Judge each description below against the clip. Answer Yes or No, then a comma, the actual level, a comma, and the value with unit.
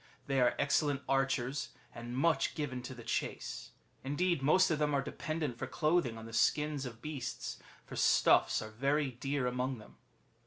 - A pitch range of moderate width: Yes, average, 3.2 semitones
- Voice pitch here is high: No, low, 135 Hz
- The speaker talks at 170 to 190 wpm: Yes, average, 180 wpm